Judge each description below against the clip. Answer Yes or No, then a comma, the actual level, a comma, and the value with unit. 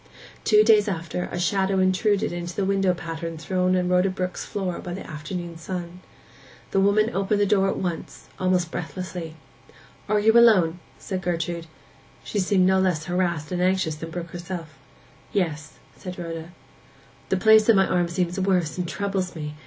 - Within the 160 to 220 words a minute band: Yes, average, 175 wpm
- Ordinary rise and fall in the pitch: No, narrow, 2.2 semitones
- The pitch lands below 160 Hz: No, medium, 180 Hz